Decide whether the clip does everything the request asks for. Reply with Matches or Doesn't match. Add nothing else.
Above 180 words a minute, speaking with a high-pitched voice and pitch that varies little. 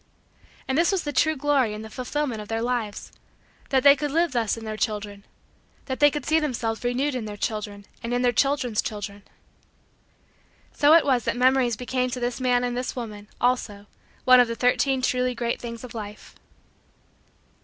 Doesn't match